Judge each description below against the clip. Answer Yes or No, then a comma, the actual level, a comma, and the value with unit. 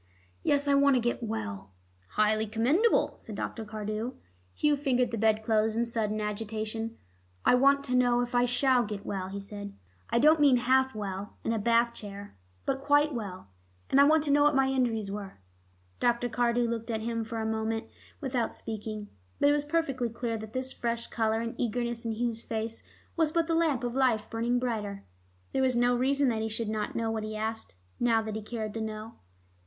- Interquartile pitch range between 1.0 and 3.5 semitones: Yes, average, 2.8 semitones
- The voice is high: Yes, high, 230 Hz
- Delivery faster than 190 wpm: Yes, average, 200 wpm